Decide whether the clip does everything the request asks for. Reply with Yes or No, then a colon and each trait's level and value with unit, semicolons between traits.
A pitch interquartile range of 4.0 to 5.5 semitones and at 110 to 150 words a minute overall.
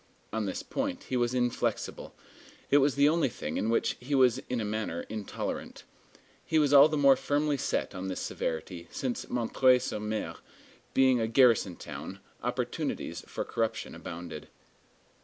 No: average, 4.4 semitones; average, 160 wpm